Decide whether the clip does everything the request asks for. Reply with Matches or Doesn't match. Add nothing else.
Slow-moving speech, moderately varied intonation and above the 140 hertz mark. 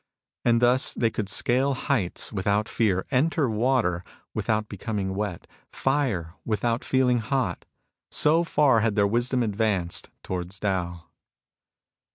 Doesn't match